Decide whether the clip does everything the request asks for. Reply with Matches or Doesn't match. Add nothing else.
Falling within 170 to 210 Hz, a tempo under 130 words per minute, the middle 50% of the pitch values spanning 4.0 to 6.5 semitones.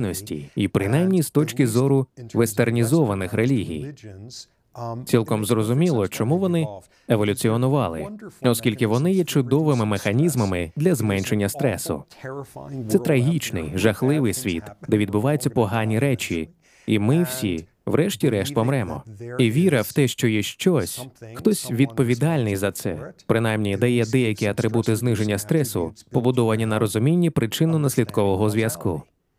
Doesn't match